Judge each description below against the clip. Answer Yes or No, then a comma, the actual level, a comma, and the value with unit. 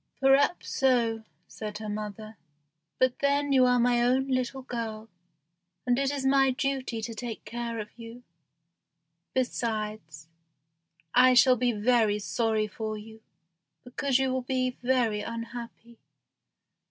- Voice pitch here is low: No, high, 240 Hz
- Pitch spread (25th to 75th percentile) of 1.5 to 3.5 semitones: Yes, average, 2.7 semitones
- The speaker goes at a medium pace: No, slow, 130 wpm